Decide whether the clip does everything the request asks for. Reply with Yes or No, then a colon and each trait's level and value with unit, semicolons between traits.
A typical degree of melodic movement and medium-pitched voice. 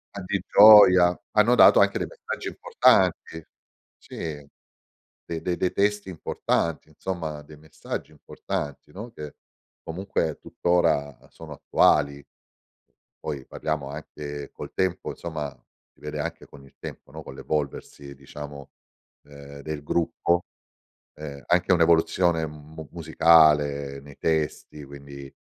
No: average, 3.3 semitones; very low, 75 Hz